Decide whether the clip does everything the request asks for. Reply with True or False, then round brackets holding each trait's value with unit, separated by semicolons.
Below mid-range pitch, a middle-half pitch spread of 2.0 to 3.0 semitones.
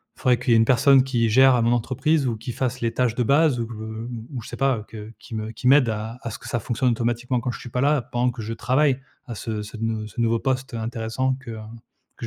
True (120 Hz; 2.4 semitones)